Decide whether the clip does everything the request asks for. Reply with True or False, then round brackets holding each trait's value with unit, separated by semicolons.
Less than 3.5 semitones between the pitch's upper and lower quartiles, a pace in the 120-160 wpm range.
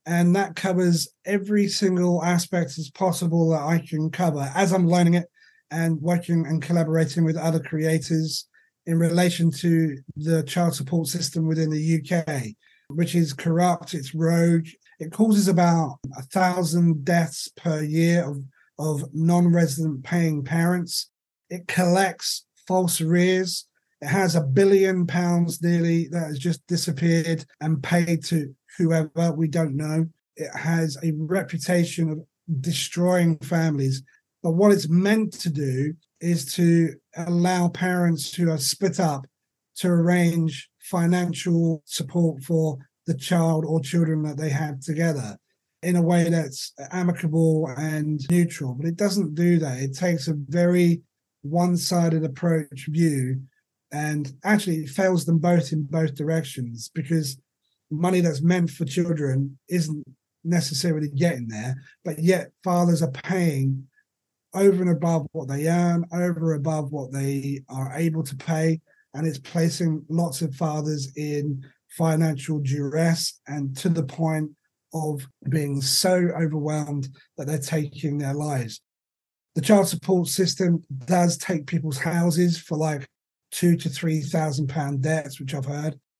True (2.5 semitones; 145 wpm)